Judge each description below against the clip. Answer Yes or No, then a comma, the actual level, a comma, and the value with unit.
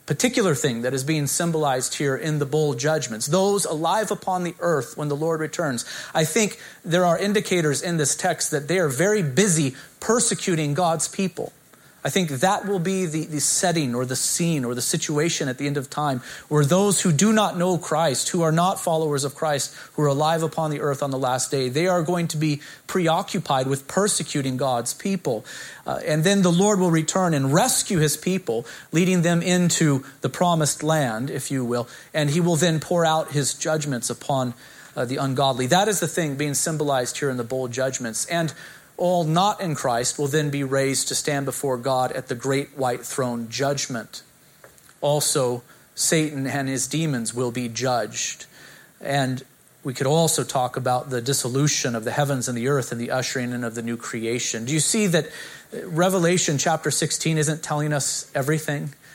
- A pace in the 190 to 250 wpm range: Yes, average, 195 wpm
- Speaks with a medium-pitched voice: Yes, medium, 150 Hz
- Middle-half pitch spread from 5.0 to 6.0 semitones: No, average, 4.2 semitones